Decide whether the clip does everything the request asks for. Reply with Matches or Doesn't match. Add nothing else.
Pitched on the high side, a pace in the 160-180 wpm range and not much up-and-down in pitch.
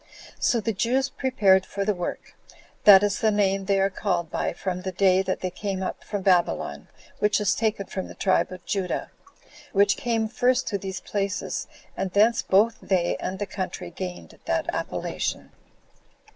Matches